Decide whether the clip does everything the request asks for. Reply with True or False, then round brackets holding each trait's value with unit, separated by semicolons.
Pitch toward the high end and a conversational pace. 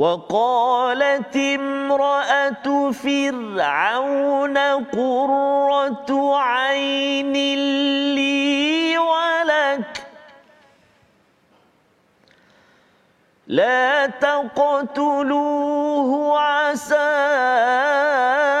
False (280 Hz; 30 wpm)